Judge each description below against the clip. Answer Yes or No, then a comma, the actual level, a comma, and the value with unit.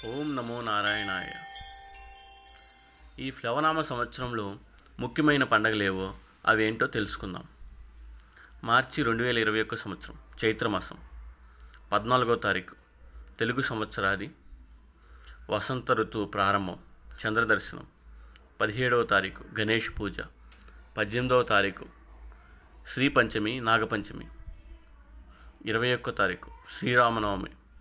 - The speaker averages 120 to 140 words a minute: No, average, 85 wpm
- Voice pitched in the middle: No, low, 100 Hz